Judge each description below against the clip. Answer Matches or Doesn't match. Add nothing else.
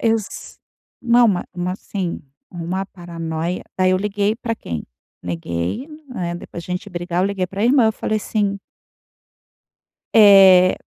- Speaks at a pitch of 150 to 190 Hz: Matches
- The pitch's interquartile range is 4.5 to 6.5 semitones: Doesn't match